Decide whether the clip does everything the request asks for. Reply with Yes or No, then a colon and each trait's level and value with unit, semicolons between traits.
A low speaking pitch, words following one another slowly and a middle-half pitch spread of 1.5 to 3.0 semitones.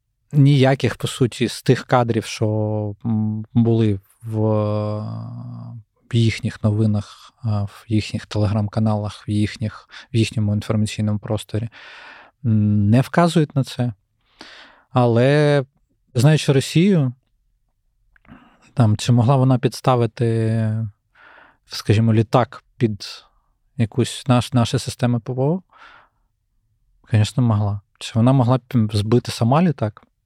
Yes: low, 115 Hz; slow, 95 wpm; narrow, 2.6 semitones